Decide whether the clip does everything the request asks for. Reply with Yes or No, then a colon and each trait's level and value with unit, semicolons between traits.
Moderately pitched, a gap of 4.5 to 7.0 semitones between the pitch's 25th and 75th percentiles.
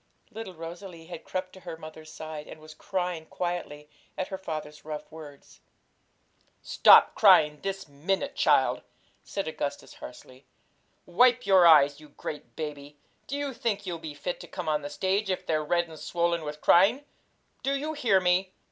No: medium, 170 Hz; average, 3.9 semitones